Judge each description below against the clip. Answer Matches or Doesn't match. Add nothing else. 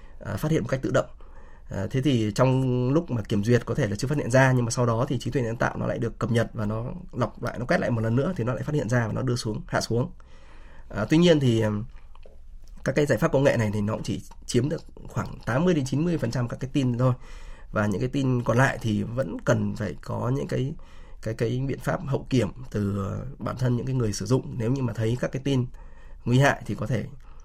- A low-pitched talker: Matches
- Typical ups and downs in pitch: Matches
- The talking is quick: Matches